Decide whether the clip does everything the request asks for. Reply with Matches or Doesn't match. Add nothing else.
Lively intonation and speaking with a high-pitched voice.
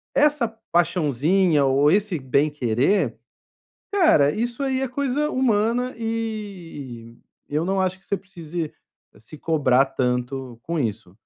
Doesn't match